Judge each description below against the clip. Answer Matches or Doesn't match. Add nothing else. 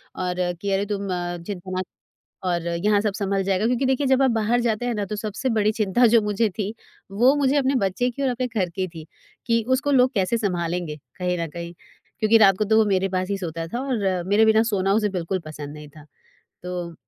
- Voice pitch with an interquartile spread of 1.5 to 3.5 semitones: Doesn't match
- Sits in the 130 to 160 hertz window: Doesn't match